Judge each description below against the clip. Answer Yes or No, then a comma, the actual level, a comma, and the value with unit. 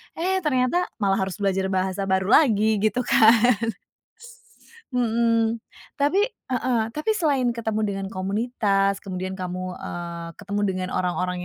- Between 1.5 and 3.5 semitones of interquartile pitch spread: No, average, 4.6 semitones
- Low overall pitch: No, high, 210 Hz